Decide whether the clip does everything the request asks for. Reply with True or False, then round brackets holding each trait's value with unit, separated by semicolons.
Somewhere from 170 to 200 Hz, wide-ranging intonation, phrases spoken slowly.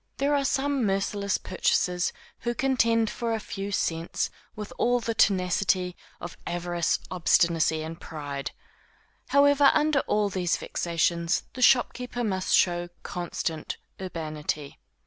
True (190 Hz; 5.7 semitones; 125 wpm)